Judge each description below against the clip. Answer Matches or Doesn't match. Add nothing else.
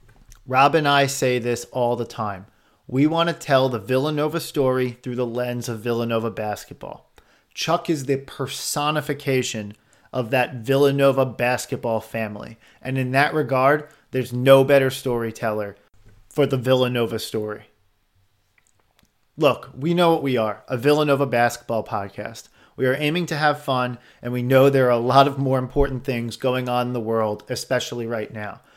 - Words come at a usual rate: Matches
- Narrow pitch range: Doesn't match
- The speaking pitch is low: Matches